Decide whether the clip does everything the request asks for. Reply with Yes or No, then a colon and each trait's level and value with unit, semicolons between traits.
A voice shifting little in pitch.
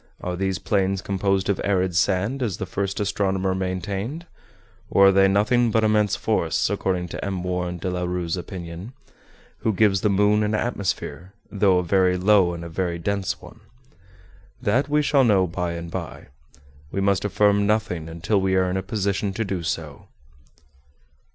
Yes: narrow, 2.2 semitones